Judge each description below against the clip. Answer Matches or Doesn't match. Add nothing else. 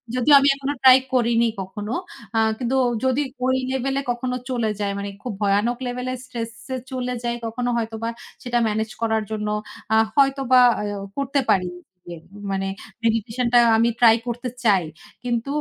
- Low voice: Doesn't match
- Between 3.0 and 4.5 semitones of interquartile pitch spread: Doesn't match